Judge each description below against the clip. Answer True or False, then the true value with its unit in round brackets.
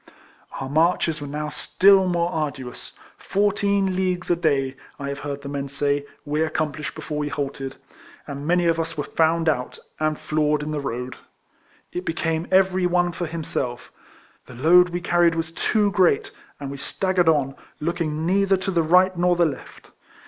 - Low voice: False (160 Hz)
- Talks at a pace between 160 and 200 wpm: True (180 wpm)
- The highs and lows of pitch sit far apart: False (3.6 semitones)